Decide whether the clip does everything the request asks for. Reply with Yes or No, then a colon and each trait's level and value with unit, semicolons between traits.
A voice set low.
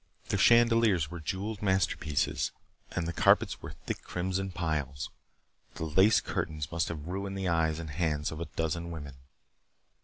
Yes: very low, 85 Hz